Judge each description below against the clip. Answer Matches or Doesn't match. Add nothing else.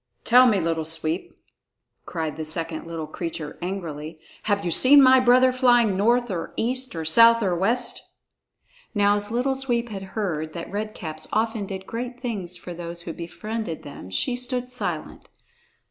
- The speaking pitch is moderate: Doesn't match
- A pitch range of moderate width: Doesn't match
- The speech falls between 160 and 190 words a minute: Matches